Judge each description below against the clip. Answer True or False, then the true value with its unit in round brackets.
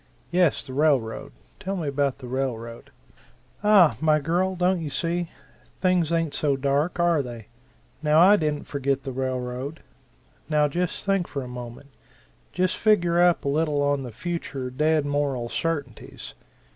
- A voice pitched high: False (150 Hz)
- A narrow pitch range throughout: False (4.4 semitones)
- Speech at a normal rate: True (155 wpm)